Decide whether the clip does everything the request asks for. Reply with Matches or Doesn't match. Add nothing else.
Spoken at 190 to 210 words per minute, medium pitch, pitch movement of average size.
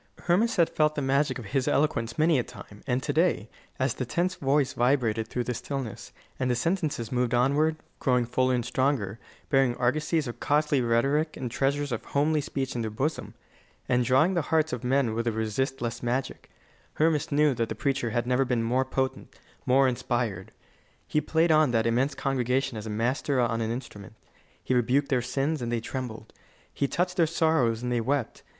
Doesn't match